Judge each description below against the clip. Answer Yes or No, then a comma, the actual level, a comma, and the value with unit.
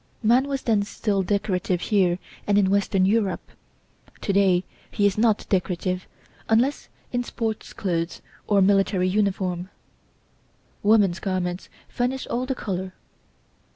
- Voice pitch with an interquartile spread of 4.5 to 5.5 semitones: No, average, 2.9 semitones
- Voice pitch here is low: No, high, 200 Hz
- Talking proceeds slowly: Yes, slow, 125 wpm